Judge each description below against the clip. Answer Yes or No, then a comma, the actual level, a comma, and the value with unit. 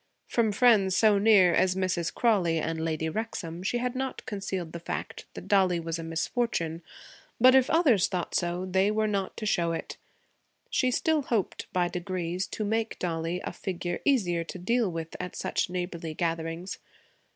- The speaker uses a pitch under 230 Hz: Yes, medium, 185 Hz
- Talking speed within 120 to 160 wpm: No, average, 175 wpm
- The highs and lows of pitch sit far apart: No, average, 4.4 semitones